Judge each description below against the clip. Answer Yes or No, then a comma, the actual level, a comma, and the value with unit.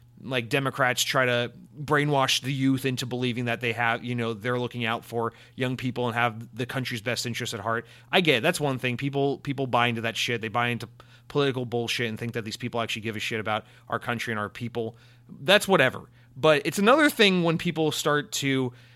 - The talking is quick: Yes, fast, 220 wpm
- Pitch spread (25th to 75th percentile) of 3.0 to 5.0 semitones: No, narrow, 2.5 semitones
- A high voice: No, low, 125 Hz